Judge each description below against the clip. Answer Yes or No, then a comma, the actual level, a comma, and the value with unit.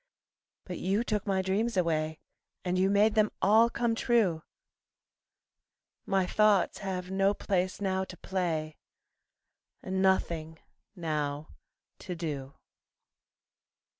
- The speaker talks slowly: Yes, slow, 110 wpm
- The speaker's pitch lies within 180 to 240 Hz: Yes, high, 190 Hz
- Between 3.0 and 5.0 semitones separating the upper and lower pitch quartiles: Yes, average, 3.3 semitones